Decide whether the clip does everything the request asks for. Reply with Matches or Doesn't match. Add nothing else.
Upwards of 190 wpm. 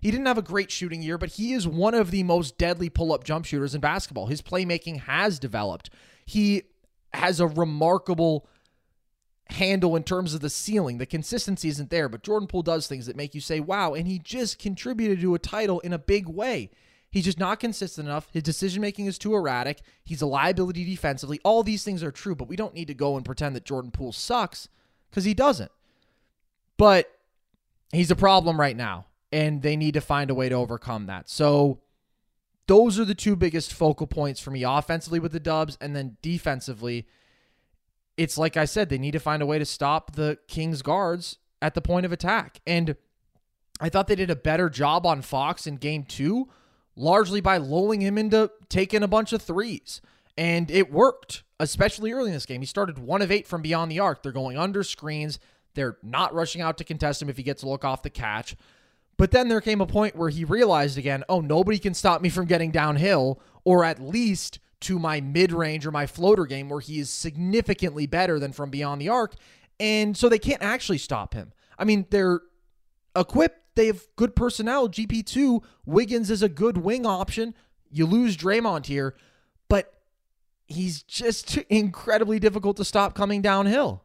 Matches